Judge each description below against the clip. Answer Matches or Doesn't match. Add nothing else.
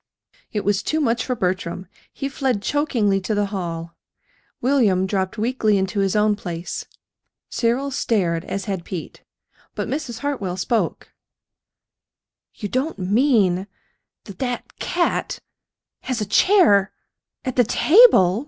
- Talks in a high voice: Matches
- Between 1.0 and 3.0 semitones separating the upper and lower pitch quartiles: Doesn't match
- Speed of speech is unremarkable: Doesn't match